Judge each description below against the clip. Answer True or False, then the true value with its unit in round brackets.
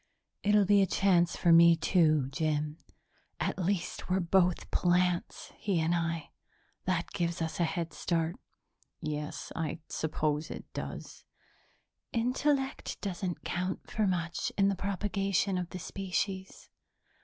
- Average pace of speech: False (130 wpm)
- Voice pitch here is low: False (175 Hz)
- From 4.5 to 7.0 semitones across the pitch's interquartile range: False (2.8 semitones)